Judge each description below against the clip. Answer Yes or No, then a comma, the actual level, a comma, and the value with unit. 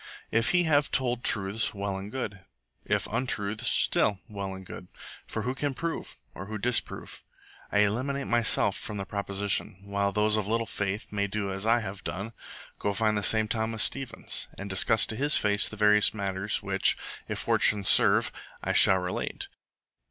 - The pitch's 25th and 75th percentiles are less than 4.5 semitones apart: Yes, narrow, 2.5 semitones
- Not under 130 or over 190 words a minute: Yes, average, 175 wpm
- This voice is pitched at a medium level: No, low, 105 Hz